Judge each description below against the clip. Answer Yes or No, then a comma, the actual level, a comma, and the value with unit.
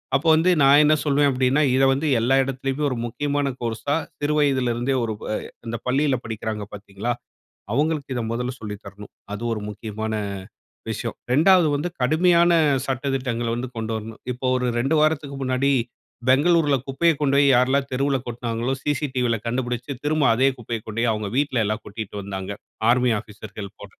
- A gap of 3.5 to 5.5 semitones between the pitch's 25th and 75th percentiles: Yes, average, 4.0 semitones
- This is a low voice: Yes, low, 130 Hz